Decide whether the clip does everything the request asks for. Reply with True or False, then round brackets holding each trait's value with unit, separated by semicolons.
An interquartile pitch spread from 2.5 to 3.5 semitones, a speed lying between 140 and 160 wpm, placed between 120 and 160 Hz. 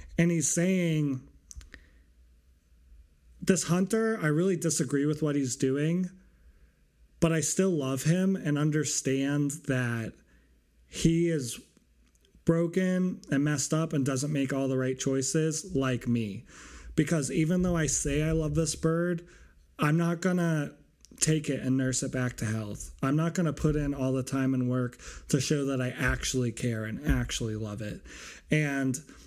False (5.5 semitones; 155 wpm; 140 Hz)